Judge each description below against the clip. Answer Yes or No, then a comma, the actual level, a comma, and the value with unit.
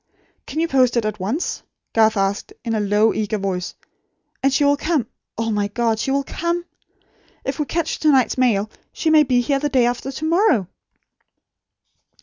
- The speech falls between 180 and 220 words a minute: Yes, average, 185 wpm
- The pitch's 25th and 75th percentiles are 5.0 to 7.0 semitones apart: Yes, average, 5.3 semitones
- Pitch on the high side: Yes, high, 245 Hz